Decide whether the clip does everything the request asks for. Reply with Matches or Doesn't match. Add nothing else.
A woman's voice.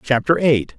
Doesn't match